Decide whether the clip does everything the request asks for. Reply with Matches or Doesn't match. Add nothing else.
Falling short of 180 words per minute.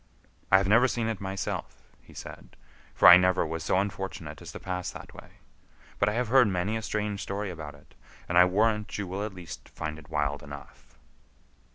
Doesn't match